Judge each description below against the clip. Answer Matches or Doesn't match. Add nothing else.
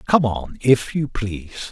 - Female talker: Doesn't match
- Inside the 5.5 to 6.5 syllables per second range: Doesn't match